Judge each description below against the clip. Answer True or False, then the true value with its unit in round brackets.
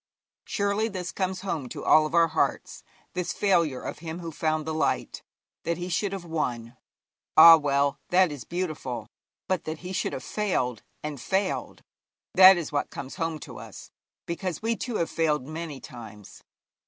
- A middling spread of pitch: True (4.0 semitones)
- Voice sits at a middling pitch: True (165 Hz)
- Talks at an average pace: True (175 wpm)